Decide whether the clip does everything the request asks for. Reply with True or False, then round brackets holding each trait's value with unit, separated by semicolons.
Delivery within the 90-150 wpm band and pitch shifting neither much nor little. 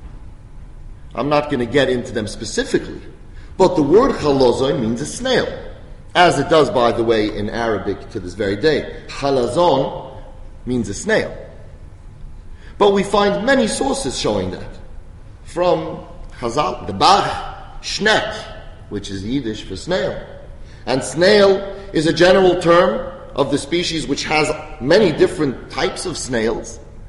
False (140 wpm; 8.7 semitones)